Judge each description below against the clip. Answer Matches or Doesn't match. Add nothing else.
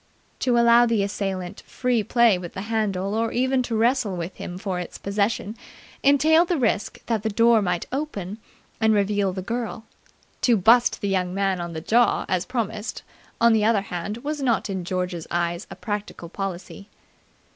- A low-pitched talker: Doesn't match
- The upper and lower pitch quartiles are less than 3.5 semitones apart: Doesn't match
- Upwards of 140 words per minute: Matches